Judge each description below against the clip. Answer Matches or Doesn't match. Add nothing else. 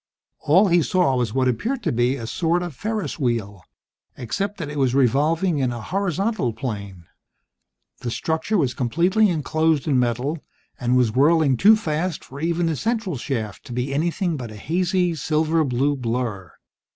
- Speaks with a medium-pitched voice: Matches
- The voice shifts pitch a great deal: Matches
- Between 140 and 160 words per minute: Doesn't match